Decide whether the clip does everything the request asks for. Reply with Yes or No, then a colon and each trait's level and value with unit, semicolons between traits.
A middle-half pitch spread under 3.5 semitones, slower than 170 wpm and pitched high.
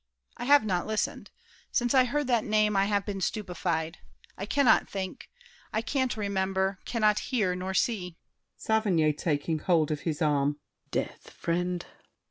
No: average, 4.1 semitones; average, 150 wpm; high, 195 Hz